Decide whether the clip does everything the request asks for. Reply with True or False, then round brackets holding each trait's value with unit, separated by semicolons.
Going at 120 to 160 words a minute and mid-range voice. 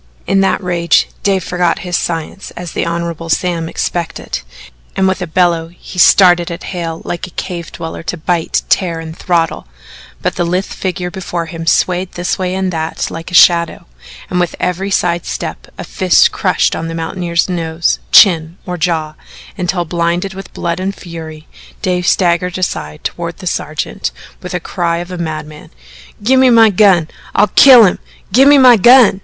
False (175 wpm; 175 Hz)